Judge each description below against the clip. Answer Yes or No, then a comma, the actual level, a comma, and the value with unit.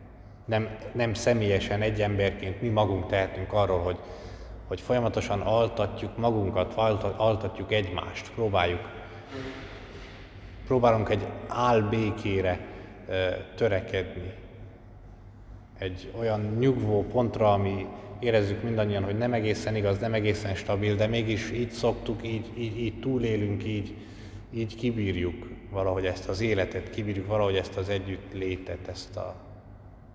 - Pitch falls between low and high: No, low, 105 Hz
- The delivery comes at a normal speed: Yes, average, 115 wpm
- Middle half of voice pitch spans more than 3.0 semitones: No, average, 2.7 semitones